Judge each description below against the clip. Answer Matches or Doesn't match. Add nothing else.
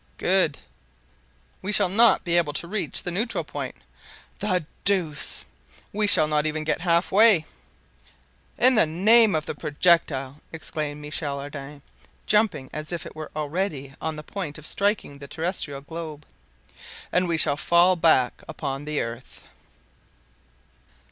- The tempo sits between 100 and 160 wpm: Matches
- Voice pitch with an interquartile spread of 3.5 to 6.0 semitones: Matches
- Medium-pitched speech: Matches